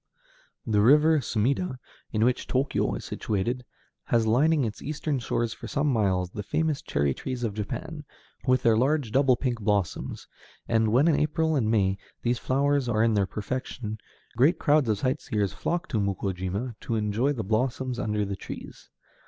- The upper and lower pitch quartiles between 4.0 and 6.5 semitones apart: Yes, average, 4.8 semitones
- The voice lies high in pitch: No, low, 120 Hz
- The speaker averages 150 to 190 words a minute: Yes, average, 170 wpm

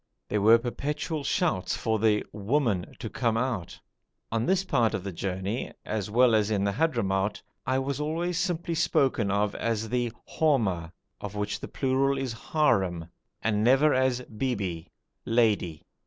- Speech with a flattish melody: No, average, 4.9 semitones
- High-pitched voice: No, low, 115 Hz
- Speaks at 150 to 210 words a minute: No, average, 140 wpm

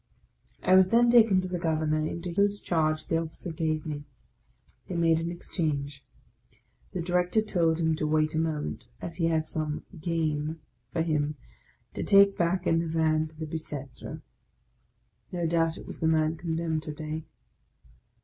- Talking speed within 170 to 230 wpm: Yes, average, 175 wpm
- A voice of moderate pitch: Yes, medium, 160 Hz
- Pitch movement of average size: No, narrow, 1.8 semitones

